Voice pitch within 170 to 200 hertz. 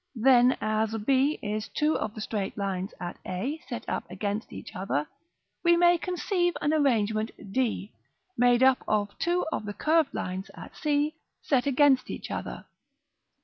No: high, 245 Hz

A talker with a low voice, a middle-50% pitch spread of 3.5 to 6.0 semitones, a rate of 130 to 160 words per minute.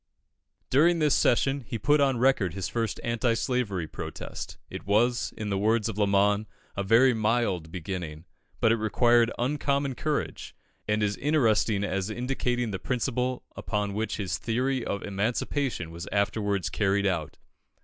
Yes: low, 110 Hz; average, 3.9 semitones; average, 150 wpm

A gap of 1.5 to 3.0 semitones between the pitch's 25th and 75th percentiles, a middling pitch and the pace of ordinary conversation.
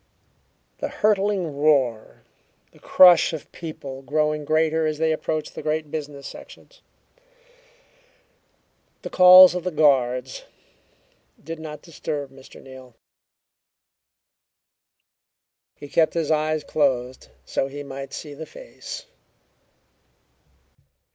No: average, 2.7 semitones; medium, 155 Hz; slow, 105 wpm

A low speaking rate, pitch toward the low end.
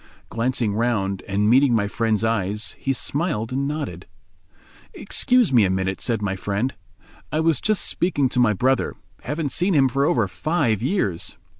No: average, 160 wpm; low, 120 Hz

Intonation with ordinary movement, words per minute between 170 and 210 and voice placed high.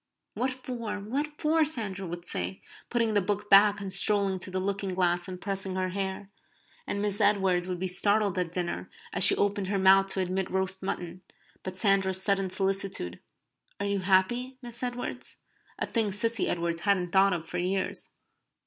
No: narrow, 1.9 semitones; average, 180 wpm; high, 195 Hz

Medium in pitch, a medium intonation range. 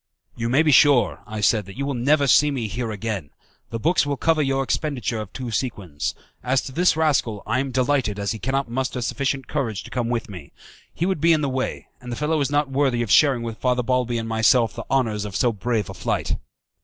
No: low, 125 Hz; average, 3.7 semitones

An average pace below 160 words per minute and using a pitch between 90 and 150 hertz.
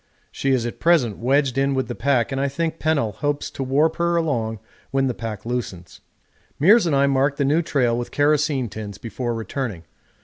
No: average, 200 wpm; low, 135 Hz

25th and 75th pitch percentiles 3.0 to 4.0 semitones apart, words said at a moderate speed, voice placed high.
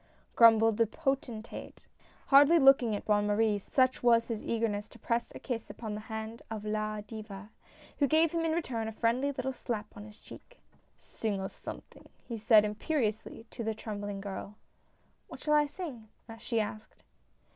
Yes: average, 3.3 semitones; average, 185 wpm; high, 225 Hz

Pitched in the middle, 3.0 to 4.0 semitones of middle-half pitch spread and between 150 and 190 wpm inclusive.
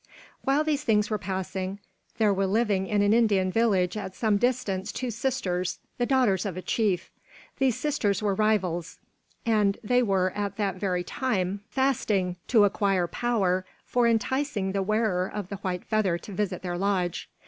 No: high, 200 Hz; average, 3.3 semitones; average, 170 wpm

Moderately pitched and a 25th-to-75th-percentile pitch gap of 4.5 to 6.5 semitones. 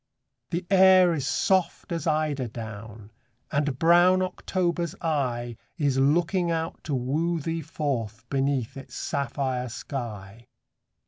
Yes: medium, 145 Hz; average, 5.3 semitones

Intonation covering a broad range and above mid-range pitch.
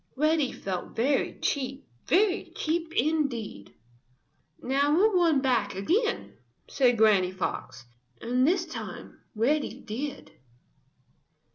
Yes: wide, 5.9 semitones; very high, 275 Hz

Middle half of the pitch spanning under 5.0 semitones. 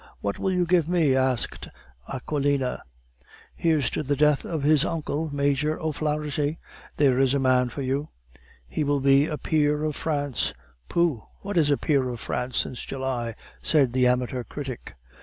Yes: average, 2.8 semitones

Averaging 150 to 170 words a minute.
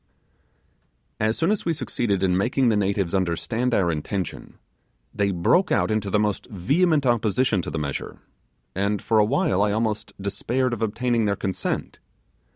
Yes: average, 165 wpm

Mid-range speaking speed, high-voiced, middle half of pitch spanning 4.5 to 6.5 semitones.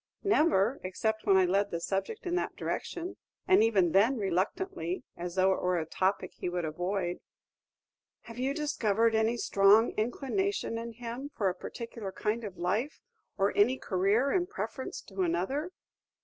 Yes: average, 165 wpm; high, 215 Hz; wide, 5.5 semitones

